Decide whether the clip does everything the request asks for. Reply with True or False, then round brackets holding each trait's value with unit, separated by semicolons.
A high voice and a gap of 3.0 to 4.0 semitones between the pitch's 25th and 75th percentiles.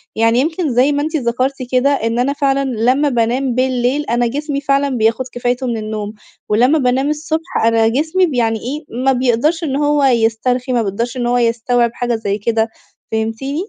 True (250 Hz; 3.4 semitones)